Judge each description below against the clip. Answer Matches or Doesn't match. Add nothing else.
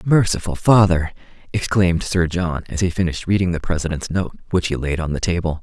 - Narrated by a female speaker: Doesn't match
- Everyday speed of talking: Matches